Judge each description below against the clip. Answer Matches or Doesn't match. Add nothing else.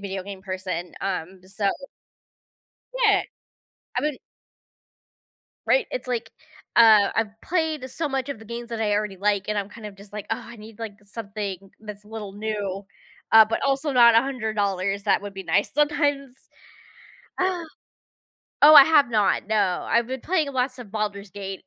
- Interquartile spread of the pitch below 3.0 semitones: Doesn't match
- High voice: Matches